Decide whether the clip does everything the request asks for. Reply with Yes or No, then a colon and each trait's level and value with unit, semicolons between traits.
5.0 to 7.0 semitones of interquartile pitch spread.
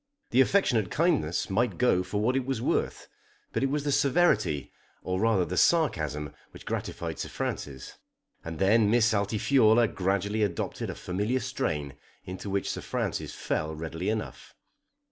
Yes: wide, 5.6 semitones